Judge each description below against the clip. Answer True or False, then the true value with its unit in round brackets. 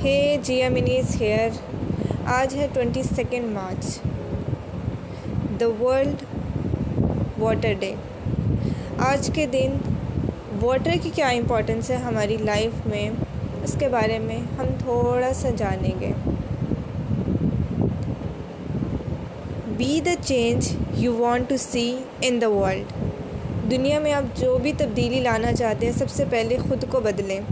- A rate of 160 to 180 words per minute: False (125 wpm)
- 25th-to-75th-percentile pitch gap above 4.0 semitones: True (4.5 semitones)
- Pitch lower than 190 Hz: False (245 Hz)